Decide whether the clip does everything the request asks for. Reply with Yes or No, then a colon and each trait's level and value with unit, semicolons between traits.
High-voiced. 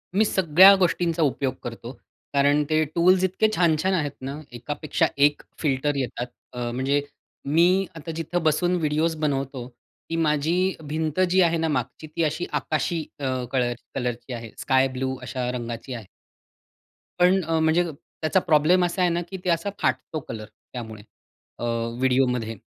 No: medium, 150 Hz